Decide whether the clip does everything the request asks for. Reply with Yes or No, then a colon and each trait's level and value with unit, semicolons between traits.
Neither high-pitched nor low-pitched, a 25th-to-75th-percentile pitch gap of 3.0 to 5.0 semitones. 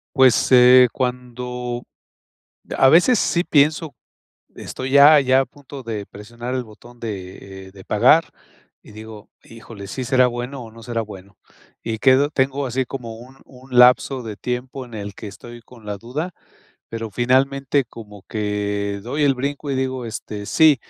No: low, 125 Hz; average, 3.3 semitones